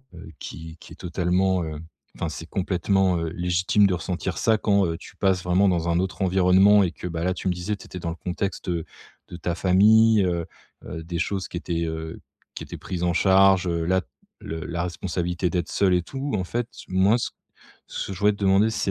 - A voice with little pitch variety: Yes, narrow, 2.1 semitones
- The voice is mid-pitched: No, very low, 90 Hz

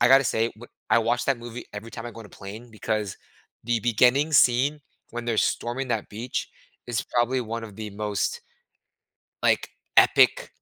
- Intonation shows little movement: Yes, narrow, 2.0 semitones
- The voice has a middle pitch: No, low, 120 Hz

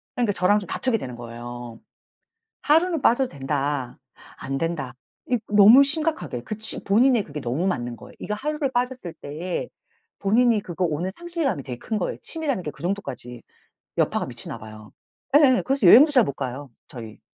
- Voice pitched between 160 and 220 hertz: Yes, medium, 185 Hz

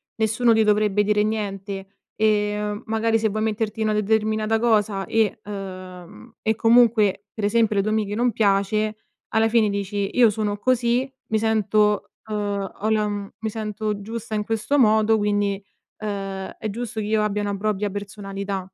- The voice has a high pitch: Yes, high, 210 Hz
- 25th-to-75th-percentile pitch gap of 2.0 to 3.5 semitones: No, narrow, 1.4 semitones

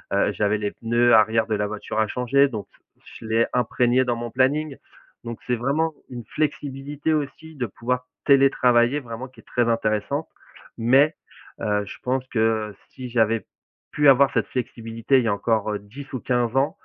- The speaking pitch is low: Yes, low, 125 Hz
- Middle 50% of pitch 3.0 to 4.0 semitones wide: Yes, average, 3.3 semitones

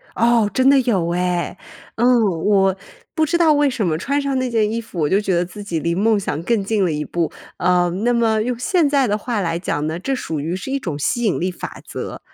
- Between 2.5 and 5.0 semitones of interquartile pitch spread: No, wide, 5.6 semitones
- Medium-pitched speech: No, high, 210 Hz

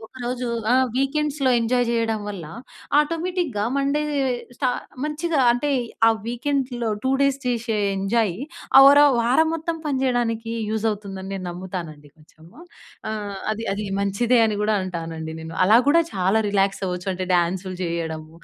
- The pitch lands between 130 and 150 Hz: No, high, 225 Hz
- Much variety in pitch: Yes, wide, 5.9 semitones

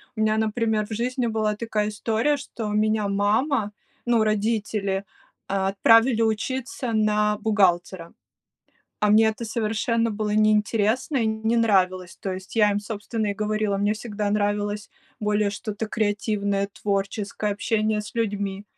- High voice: Yes, high, 215 Hz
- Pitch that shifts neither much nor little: No, narrow, 1.5 semitones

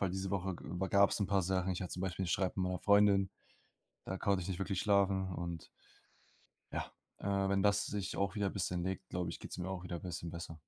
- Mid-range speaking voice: No, very low, 95 Hz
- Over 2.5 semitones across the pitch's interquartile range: No, narrow, 1.6 semitones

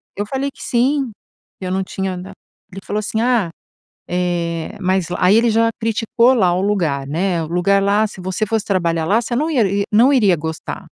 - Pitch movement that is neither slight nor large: Yes, average, 4.2 semitones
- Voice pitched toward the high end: Yes, high, 195 Hz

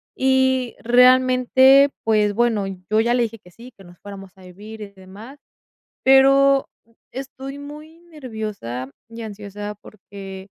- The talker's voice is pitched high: Yes, high, 230 Hz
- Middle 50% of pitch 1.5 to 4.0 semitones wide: No, average, 4.7 semitones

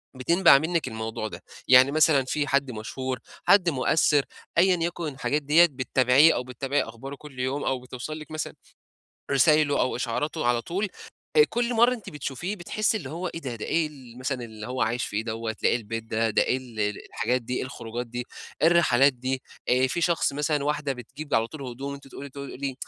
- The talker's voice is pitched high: No, low, 135 Hz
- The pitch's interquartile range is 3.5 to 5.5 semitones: Yes, average, 3.8 semitones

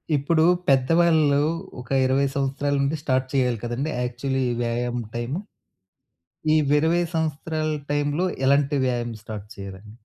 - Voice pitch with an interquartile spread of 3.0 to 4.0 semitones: Yes, average, 3.6 semitones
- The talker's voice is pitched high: No, low, 135 Hz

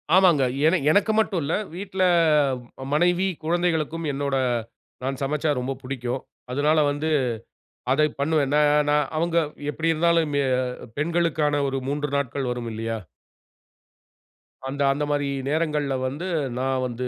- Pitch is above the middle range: No, medium, 150 Hz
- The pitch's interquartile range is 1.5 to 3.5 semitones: Yes, average, 3.2 semitones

